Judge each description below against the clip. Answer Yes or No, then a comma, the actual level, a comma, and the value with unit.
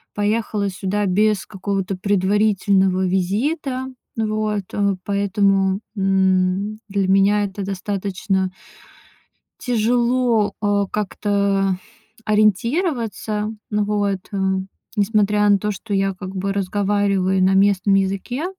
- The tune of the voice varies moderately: No, narrow, 1.6 semitones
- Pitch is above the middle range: Yes, high, 200 Hz